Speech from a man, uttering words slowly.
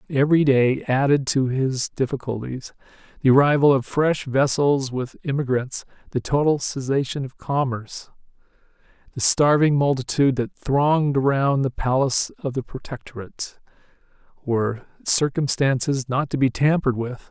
Yes: male; slow, 125 wpm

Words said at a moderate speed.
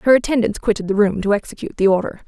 No: fast, 240 wpm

